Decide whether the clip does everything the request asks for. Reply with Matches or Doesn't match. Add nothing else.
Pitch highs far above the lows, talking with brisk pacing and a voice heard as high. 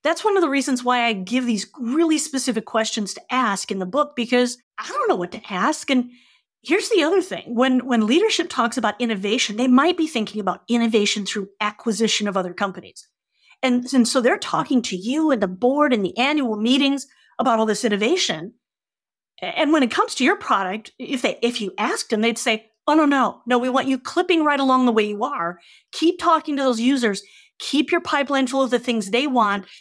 Doesn't match